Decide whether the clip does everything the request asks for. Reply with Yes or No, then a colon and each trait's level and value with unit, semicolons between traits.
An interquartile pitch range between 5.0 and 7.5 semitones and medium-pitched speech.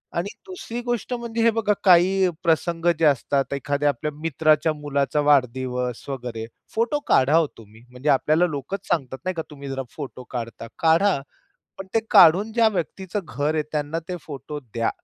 Yes: wide, 5.5 semitones; medium, 155 Hz